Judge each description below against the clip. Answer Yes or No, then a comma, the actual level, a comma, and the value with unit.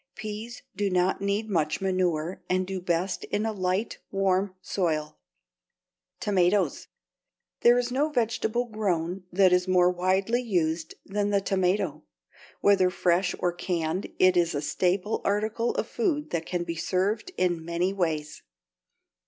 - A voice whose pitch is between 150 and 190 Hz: Yes, medium, 185 Hz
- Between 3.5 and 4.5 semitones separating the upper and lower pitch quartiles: No, average, 2.7 semitones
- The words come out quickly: No, average, 145 wpm